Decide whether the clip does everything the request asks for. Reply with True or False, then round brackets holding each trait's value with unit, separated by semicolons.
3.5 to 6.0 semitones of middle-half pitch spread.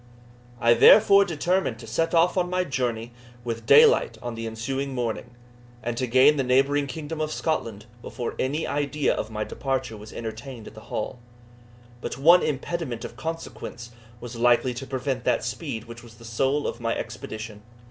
True (4.2 semitones)